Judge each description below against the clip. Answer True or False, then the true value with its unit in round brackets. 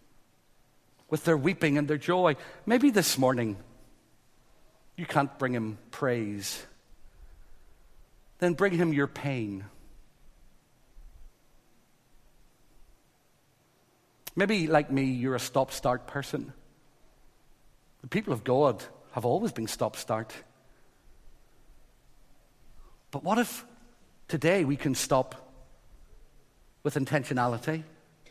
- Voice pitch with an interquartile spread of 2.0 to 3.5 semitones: False (4.8 semitones)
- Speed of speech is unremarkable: False (95 wpm)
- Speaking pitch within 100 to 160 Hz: True (140 Hz)